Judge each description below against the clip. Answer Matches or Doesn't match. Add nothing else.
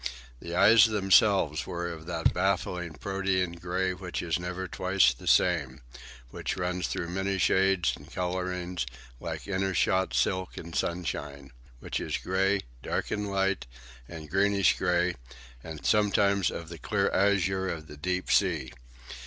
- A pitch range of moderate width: Doesn't match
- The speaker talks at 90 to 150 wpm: Matches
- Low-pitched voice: Matches